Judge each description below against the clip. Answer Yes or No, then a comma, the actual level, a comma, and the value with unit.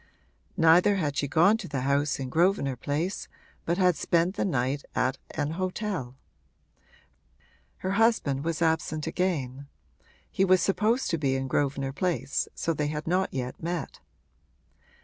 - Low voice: No, medium, 160 Hz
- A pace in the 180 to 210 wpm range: No, average, 150 wpm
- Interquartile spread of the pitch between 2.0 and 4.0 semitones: No, average, 4.8 semitones